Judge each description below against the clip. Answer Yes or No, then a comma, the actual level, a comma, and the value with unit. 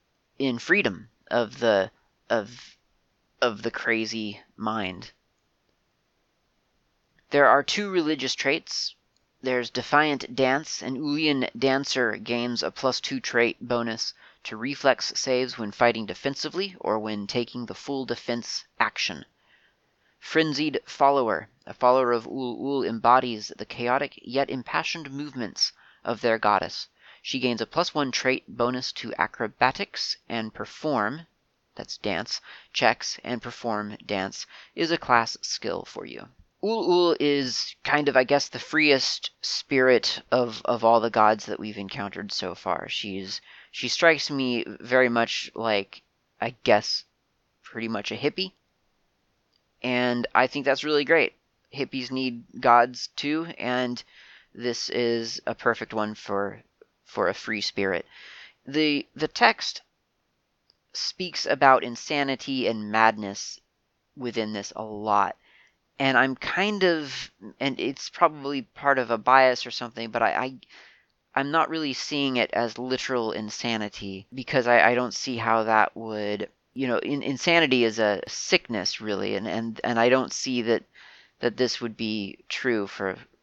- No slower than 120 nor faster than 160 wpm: Yes, average, 140 wpm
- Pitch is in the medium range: No, low, 125 Hz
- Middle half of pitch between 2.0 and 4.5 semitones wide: Yes, average, 3.5 semitones